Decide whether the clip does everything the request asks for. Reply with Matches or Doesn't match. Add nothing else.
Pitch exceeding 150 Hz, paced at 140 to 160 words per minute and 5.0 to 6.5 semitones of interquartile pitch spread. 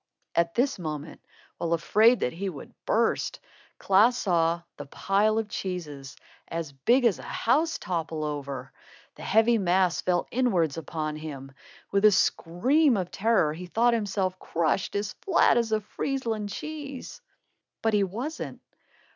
Matches